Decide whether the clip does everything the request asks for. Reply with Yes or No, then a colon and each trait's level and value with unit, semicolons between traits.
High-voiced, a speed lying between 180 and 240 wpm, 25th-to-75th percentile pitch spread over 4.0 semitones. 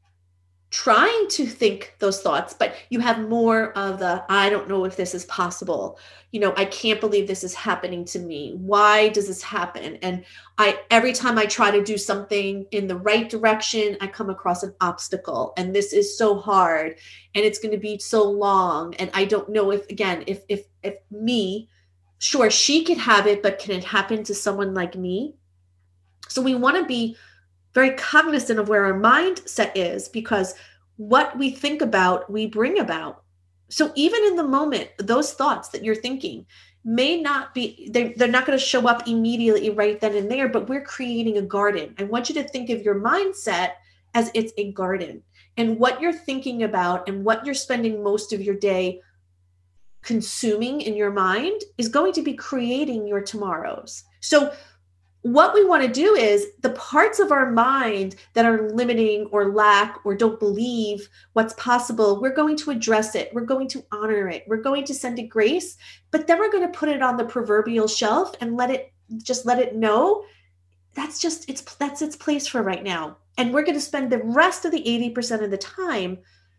Yes: high, 215 Hz; average, 195 wpm; average, 4.7 semitones